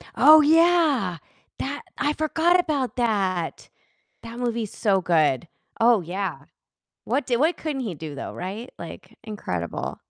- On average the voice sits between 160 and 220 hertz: No, high, 230 Hz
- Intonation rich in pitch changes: Yes, wide, 7.9 semitones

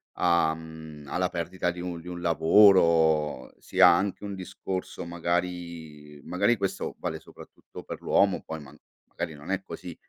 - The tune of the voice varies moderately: No, narrow, 2.3 semitones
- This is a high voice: No, very low, 85 Hz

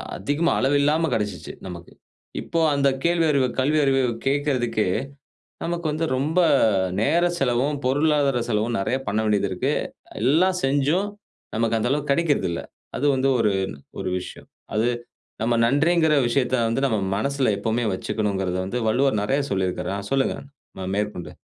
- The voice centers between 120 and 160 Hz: Yes, low, 135 Hz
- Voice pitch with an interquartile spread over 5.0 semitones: Yes, wide, 5.4 semitones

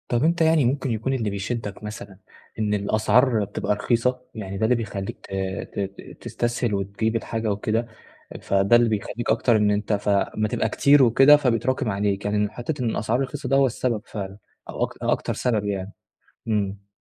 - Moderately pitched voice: No, low, 110 Hz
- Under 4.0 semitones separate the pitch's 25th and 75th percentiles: Yes, average, 3.0 semitones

